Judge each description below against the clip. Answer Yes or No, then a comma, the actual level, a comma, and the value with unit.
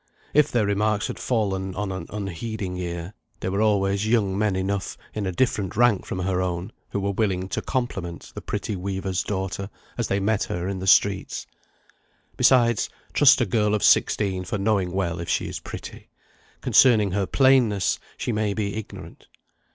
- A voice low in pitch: Yes, low, 100 Hz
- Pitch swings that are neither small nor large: No, narrow, 2.3 semitones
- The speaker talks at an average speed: Yes, average, 175 wpm